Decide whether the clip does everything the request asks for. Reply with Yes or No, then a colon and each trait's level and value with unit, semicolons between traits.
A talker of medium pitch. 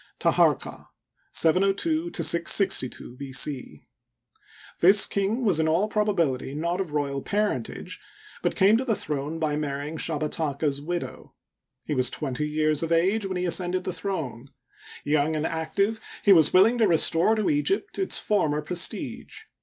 Yes: medium, 165 Hz